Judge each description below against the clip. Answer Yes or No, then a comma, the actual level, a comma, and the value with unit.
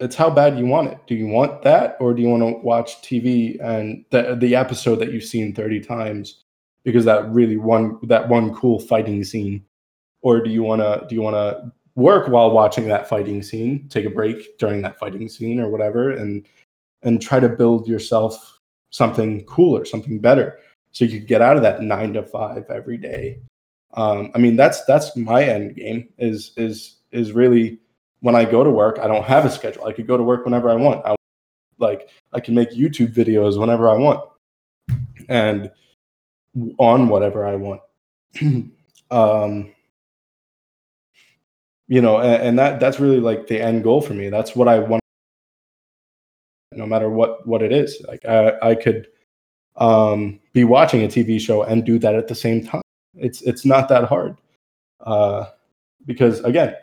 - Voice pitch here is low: Yes, low, 115 Hz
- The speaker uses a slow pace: No, average, 185 wpm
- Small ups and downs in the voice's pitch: Yes, narrow, 2.1 semitones